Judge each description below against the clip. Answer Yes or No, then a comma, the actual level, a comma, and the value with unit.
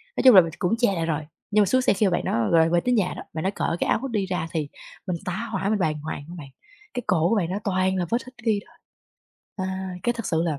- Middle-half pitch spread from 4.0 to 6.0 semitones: Yes, average, 4.3 semitones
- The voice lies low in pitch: No, high, 190 Hz